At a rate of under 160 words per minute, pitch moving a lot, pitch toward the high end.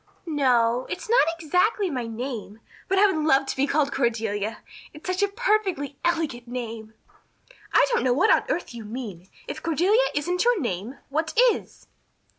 No: average, 180 wpm; wide, 7.4 semitones; very high, 280 Hz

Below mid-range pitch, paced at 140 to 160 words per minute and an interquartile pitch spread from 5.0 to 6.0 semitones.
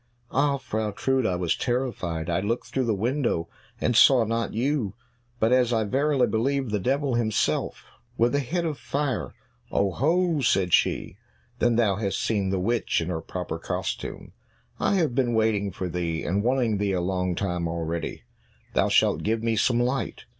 No: low, 115 Hz; average, 175 wpm; wide, 5.4 semitones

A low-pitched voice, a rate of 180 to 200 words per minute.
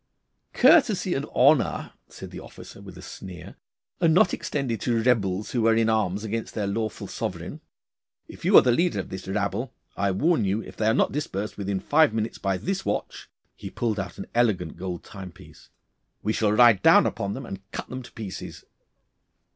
Yes: low, 110 Hz; average, 195 wpm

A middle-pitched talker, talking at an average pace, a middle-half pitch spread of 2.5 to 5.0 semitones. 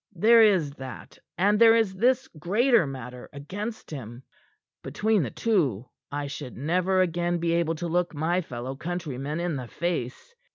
No: medium, 170 Hz; average, 160 wpm; wide, 5.6 semitones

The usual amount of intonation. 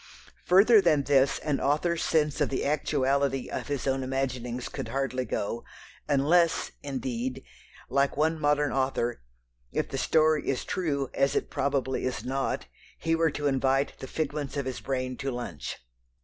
No: narrow, 2.3 semitones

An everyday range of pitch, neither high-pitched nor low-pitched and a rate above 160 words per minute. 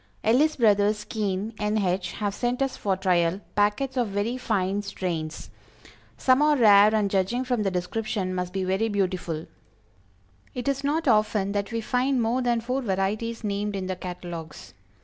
No: average, 4.0 semitones; high, 205 Hz; average, 170 wpm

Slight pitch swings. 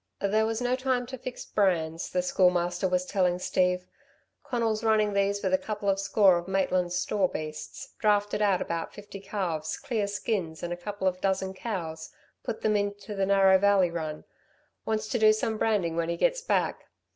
No: average, 3.1 semitones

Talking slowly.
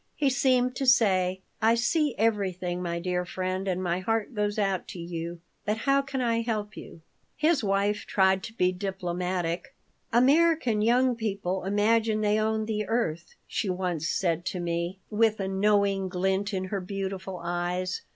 No: average, 165 wpm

